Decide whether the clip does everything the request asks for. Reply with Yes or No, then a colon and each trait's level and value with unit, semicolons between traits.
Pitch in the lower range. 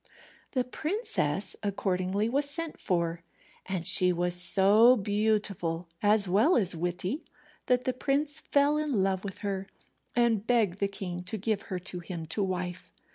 No: high, 200 Hz